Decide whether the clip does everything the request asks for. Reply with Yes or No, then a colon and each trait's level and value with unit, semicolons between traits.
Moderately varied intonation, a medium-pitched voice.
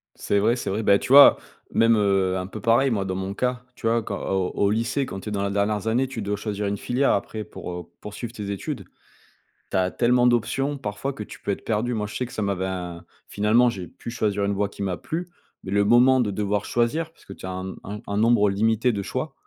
No: average, 3.3 semitones; low, 105 Hz